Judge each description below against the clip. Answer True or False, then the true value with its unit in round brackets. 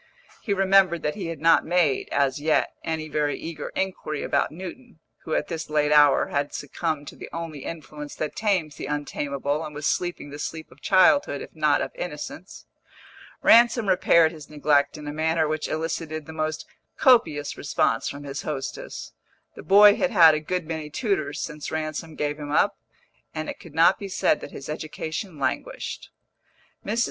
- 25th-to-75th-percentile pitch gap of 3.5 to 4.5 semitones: False (2.9 semitones)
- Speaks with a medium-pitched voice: True (155 Hz)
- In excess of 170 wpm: True (180 wpm)